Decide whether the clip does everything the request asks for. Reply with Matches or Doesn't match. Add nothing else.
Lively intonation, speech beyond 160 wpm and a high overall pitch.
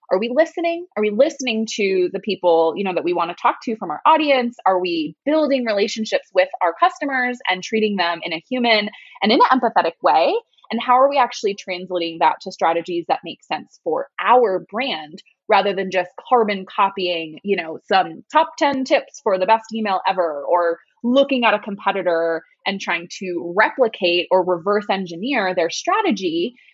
Matches